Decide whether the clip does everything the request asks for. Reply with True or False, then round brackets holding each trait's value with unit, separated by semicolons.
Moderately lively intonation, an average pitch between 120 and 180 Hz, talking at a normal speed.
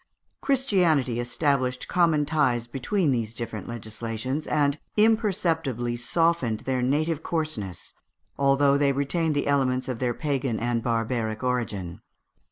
False (4.6 semitones; 135 Hz; 120 wpm)